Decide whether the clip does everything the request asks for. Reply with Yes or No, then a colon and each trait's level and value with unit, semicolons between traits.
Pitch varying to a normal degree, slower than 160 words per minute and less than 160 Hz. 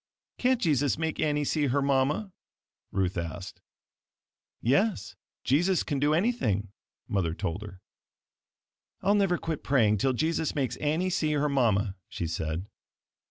No: wide, 7.7 semitones; slow, 135 wpm; medium, 140 Hz